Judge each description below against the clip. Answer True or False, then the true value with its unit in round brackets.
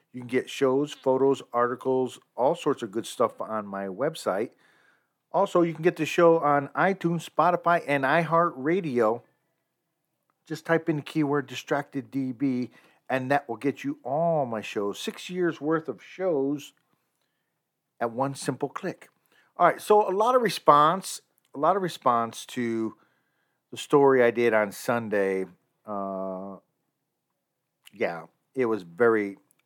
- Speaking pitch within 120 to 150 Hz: True (140 Hz)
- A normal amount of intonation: False (5.7 semitones)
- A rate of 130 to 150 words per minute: True (145 wpm)